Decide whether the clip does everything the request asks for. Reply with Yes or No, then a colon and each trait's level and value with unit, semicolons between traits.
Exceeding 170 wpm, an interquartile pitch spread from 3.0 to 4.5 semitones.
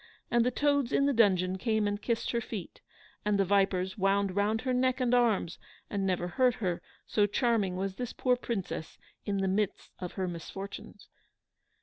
Yes: average, 185 wpm; average, 3.9 semitones